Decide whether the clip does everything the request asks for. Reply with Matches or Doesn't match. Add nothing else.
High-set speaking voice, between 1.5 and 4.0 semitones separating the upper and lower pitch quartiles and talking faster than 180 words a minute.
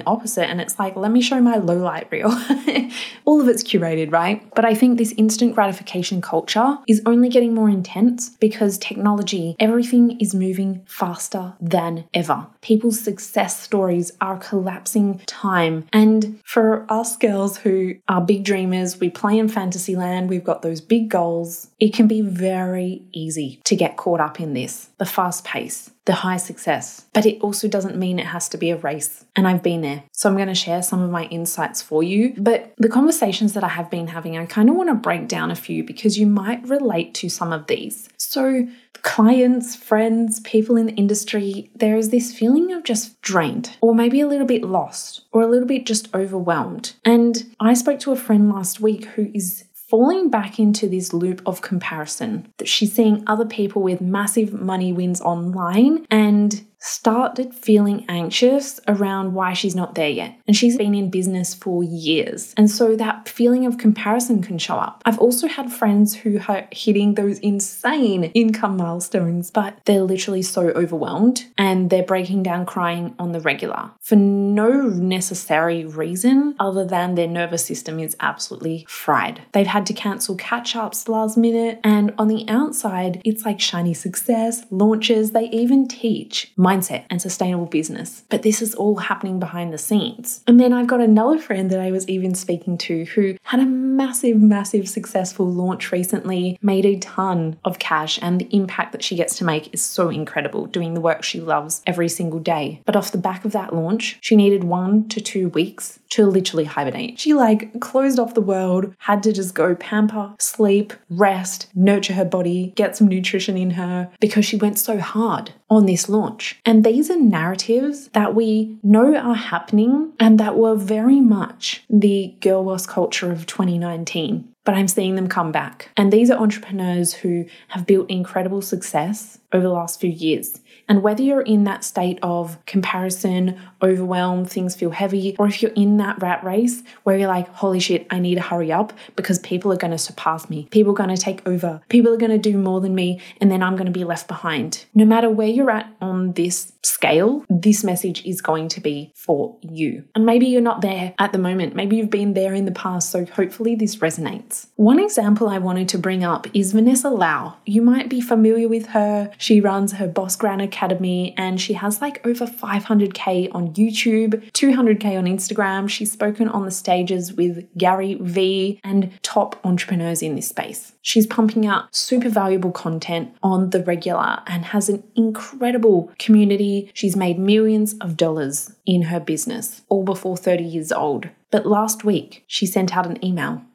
Matches